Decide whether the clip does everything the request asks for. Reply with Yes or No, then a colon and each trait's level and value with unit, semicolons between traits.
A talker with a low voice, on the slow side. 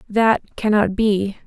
No: high, 210 Hz; slow, 125 wpm